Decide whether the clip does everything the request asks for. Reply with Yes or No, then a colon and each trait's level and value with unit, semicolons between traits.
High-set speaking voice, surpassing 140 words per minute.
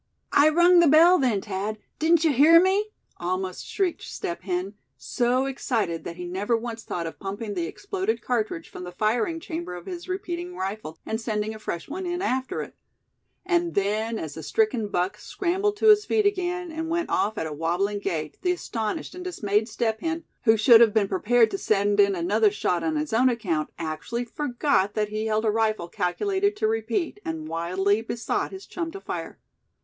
Yes: high, 225 Hz; average, 195 wpm